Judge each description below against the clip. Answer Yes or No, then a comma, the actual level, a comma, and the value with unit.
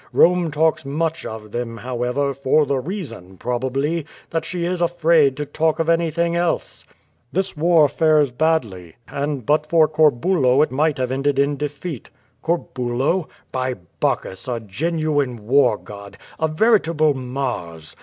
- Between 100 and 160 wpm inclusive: Yes, average, 145 wpm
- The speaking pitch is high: No, medium, 145 Hz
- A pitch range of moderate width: Yes, average, 4.4 semitones